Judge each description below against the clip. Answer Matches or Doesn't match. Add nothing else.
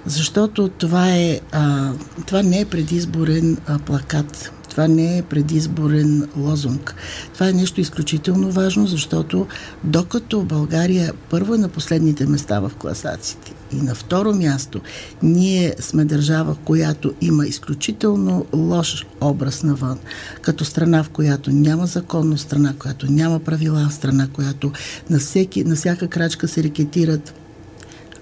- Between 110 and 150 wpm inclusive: Matches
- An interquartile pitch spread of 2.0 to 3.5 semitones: Matches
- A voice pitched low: Doesn't match